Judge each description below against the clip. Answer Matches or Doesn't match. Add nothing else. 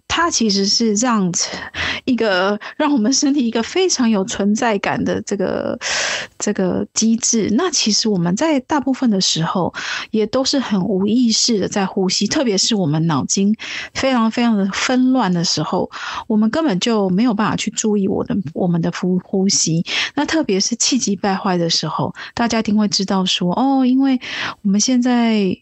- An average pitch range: Matches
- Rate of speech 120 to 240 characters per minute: Doesn't match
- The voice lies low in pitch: Doesn't match